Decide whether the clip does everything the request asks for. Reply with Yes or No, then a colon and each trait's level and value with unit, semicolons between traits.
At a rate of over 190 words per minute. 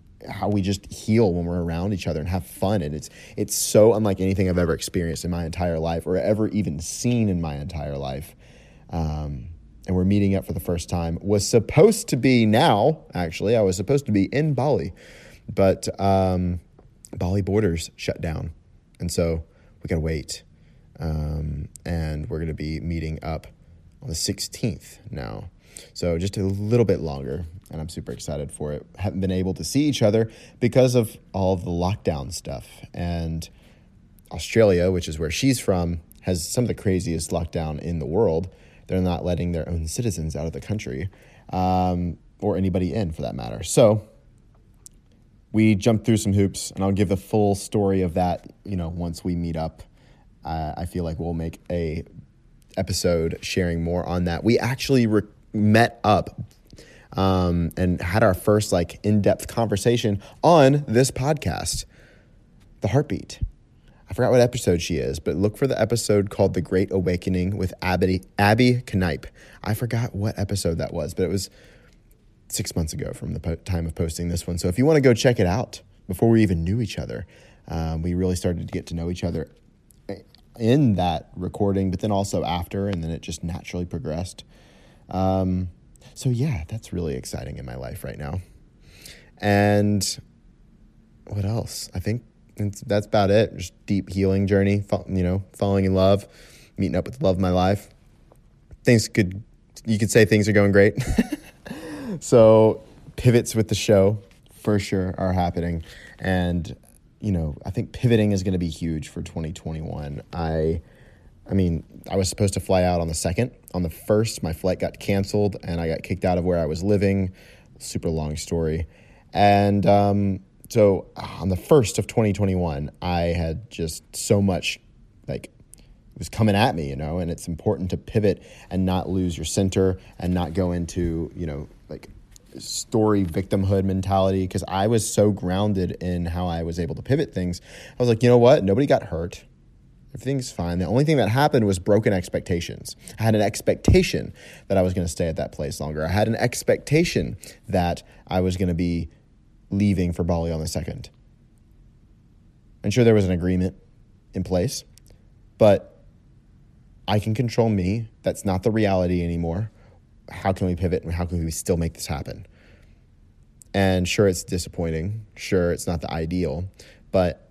No: average, 180 wpm